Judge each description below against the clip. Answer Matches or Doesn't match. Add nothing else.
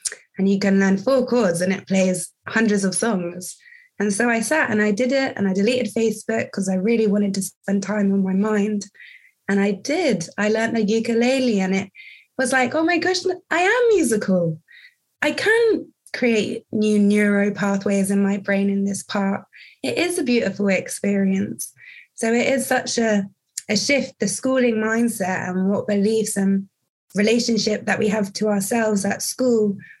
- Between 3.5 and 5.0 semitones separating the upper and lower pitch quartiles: Matches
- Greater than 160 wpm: Matches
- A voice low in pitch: Doesn't match